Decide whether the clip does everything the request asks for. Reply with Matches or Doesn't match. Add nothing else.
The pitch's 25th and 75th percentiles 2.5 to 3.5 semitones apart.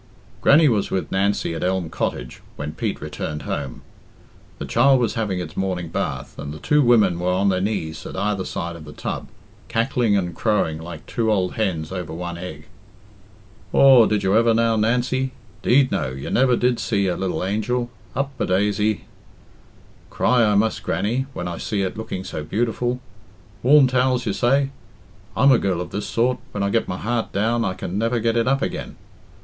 Doesn't match